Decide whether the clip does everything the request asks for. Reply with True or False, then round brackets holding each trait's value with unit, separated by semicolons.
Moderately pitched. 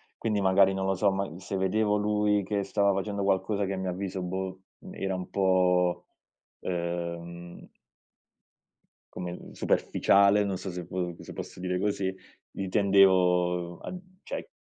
False (95 Hz)